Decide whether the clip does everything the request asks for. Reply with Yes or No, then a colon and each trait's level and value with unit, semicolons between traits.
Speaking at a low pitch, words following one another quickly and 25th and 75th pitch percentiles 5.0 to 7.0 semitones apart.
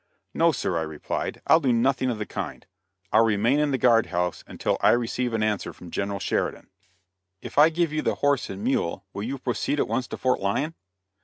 Yes: low, 120 Hz; fast, 215 wpm; wide, 5.4 semitones